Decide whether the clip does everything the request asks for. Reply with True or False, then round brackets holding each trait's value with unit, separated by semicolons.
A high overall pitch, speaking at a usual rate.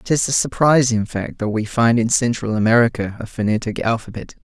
False (115 Hz; 190 wpm)